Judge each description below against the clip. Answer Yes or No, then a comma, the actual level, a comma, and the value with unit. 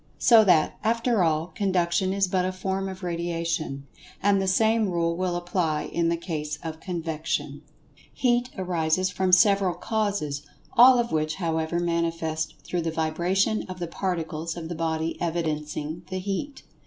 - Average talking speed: Yes, average, 155 wpm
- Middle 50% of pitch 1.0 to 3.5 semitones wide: Yes, average, 2.9 semitones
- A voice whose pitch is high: No, medium, 175 Hz